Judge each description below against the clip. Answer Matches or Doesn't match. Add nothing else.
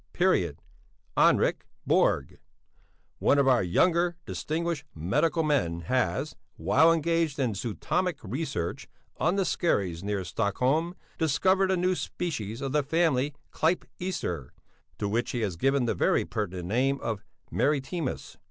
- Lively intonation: Matches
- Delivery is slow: Matches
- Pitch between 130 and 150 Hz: Matches